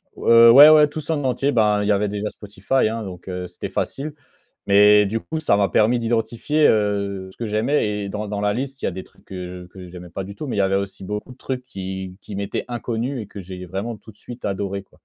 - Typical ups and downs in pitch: Yes, average, 3.6 semitones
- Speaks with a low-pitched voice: Yes, low, 105 Hz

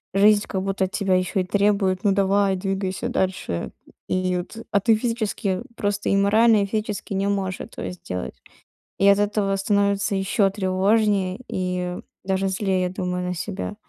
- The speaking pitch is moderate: No, high, 195 Hz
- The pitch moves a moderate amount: No, narrow, 1.6 semitones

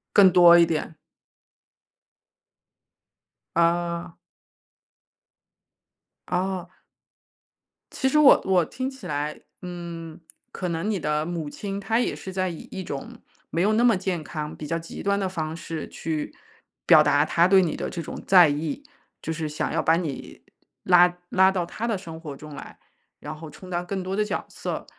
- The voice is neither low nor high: Yes, medium, 175 Hz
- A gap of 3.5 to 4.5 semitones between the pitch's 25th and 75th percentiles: No, average, 3.0 semitones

